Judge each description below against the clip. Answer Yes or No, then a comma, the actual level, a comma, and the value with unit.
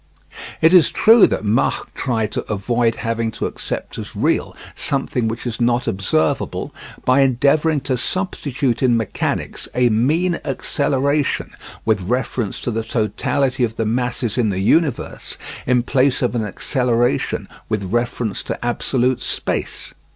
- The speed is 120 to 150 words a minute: Yes, average, 145 wpm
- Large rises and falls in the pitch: No, average, 3.2 semitones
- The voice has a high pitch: No, low, 120 Hz